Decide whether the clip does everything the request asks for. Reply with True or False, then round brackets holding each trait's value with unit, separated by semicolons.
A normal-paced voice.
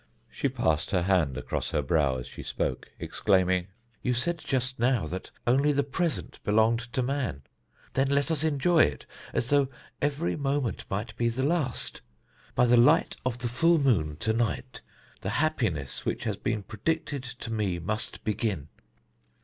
True (165 wpm)